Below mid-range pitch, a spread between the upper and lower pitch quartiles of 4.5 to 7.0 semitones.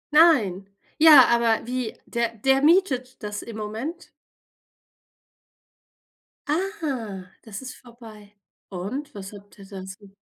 No: high, 230 Hz; average, 4.9 semitones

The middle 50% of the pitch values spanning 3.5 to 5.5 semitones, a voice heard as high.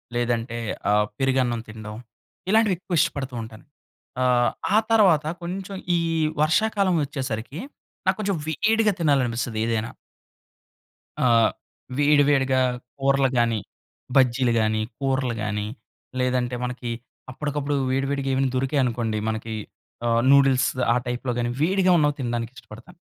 No: average, 4.0 semitones; low, 130 Hz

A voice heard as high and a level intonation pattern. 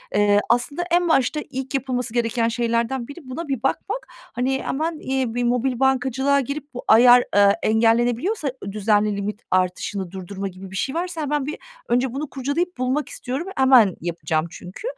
No: very high, 250 Hz; average, 4.6 semitones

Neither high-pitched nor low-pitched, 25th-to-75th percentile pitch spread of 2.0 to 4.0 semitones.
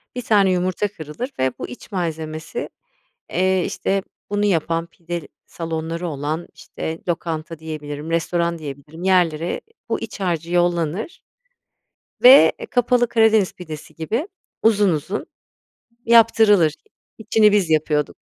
No: medium, 170 Hz; average, 4.4 semitones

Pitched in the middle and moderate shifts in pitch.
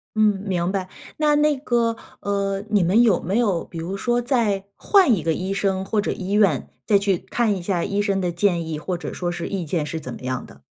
No: high, 195 Hz; average, 3.5 semitones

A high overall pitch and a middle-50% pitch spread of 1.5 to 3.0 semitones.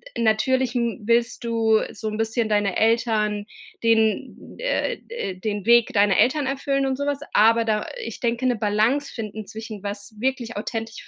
Yes: high, 225 Hz; narrow, 2.5 semitones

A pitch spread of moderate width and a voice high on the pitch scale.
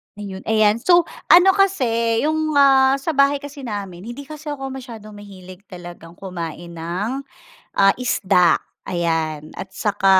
No: wide, 7.0 semitones; high, 215 Hz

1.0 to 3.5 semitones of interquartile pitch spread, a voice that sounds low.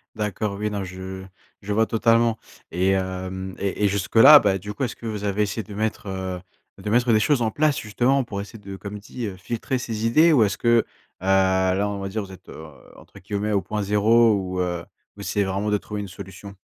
Yes: average, 2.8 semitones; low, 105 Hz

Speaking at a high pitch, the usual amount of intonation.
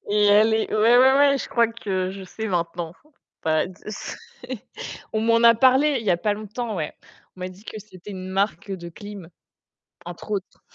Yes: high, 210 Hz; average, 3.7 semitones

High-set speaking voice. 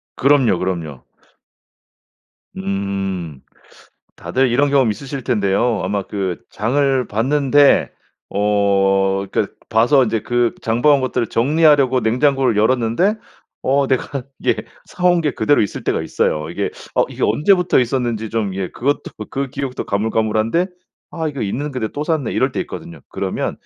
No: low, 120 Hz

